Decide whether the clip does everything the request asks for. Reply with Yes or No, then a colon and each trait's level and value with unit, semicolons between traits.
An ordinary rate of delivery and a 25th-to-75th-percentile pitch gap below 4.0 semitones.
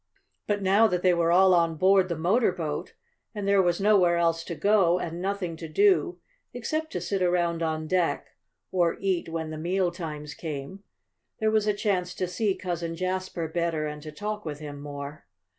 Yes: average, 190 wpm; average, 3.1 semitones